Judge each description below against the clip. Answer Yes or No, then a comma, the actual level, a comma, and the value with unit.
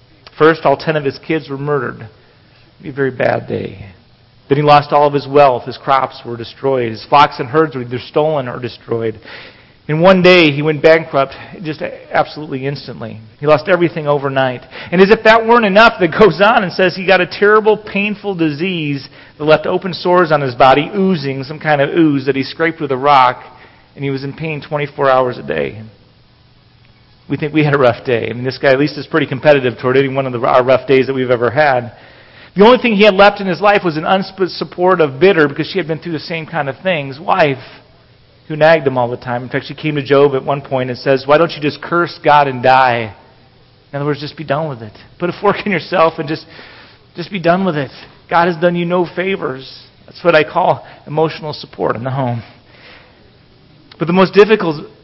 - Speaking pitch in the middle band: Yes, medium, 145 Hz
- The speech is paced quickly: Yes, fast, 225 wpm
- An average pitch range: Yes, average, 4.6 semitones